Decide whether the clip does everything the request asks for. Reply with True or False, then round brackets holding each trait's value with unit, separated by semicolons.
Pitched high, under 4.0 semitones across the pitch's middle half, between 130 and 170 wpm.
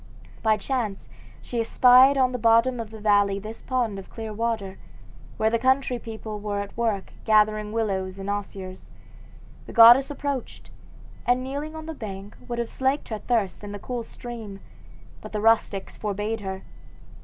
True (225 Hz; 3.2 semitones; 165 wpm)